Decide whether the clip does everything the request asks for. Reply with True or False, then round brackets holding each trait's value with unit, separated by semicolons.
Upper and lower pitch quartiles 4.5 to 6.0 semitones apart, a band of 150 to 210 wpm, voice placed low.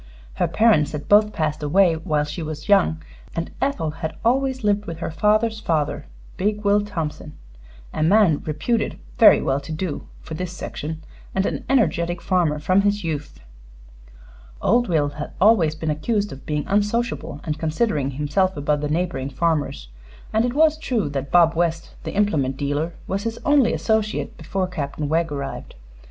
False (5.6 semitones; 170 wpm; 165 Hz)